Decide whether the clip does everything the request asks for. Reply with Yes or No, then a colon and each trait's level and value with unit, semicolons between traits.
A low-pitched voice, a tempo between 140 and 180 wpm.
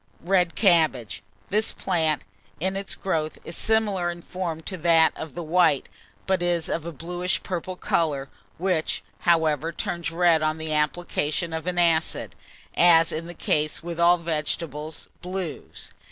No: medium, 170 Hz; average, 150 wpm